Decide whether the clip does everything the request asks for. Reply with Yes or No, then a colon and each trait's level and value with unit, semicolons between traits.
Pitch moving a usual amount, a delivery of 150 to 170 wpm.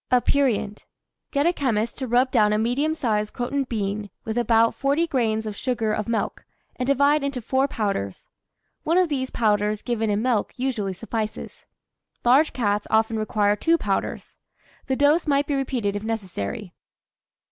Yes: average, 4.4 semitones; average, 160 wpm